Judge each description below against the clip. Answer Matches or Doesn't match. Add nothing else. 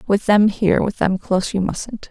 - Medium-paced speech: Doesn't match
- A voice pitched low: Doesn't match